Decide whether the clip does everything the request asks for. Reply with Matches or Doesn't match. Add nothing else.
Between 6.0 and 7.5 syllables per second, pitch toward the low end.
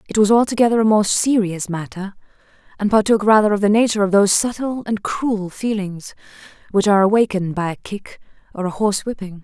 Doesn't match